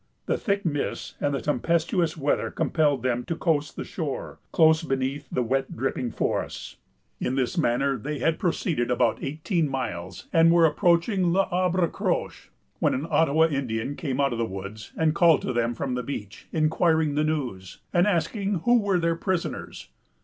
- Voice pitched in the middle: Yes, medium, 150 Hz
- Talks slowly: No, average, 170 wpm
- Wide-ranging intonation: No, average, 4.5 semitones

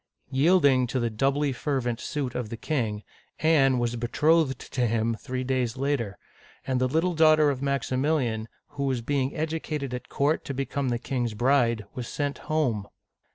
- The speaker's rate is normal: Yes, average, 170 wpm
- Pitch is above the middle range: No, low, 130 Hz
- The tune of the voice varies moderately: Yes, average, 3.3 semitones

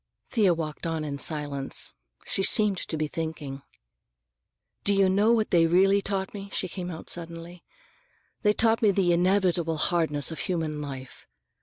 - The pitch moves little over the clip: No, average, 3.8 semitones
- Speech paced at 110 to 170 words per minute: Yes, average, 160 wpm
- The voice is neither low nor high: Yes, medium, 175 Hz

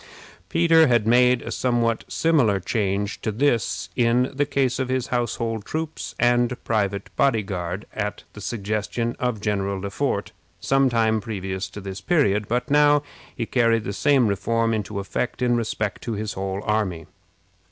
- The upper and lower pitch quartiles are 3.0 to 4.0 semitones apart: Yes, average, 3.6 semitones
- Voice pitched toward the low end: Yes, low, 115 Hz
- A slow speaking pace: No, average, 165 wpm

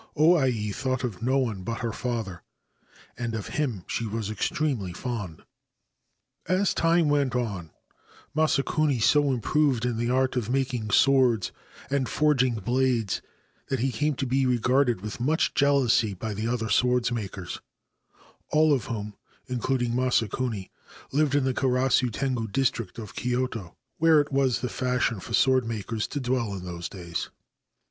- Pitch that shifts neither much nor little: Yes, average, 3.3 semitones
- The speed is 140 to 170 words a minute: Yes, average, 150 wpm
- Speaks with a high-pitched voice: No, low, 125 Hz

